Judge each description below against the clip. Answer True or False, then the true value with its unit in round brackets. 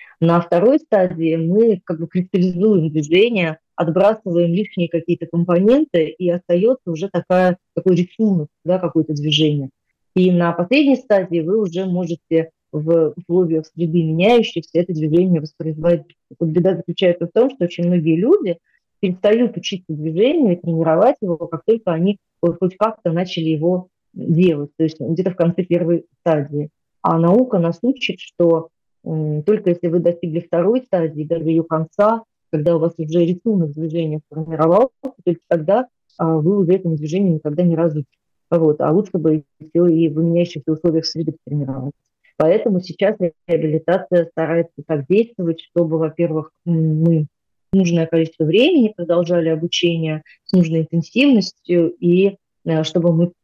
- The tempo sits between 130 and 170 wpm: True (145 wpm)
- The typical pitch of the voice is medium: True (170 Hz)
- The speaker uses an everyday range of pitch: False (2.1 semitones)